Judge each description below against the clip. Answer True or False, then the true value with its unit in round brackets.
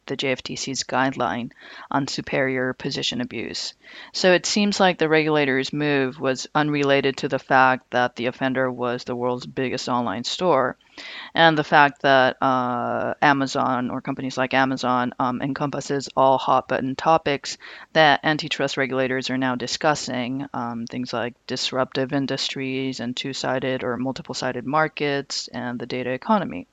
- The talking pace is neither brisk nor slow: True (145 wpm)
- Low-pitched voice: True (130 Hz)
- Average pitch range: False (1.8 semitones)